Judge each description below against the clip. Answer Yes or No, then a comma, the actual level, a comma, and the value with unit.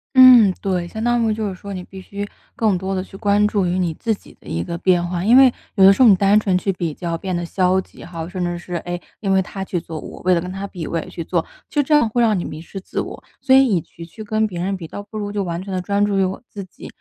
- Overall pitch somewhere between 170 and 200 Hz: Yes, high, 190 Hz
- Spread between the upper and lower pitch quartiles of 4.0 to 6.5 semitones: No, average, 2.9 semitones